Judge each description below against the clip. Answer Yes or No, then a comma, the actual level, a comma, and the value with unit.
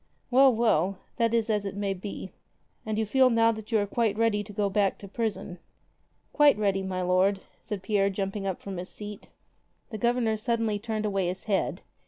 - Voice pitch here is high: Yes, high, 210 Hz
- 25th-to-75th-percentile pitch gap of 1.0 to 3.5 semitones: Yes, narrow, 2.5 semitones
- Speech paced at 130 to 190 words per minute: No, average, 200 wpm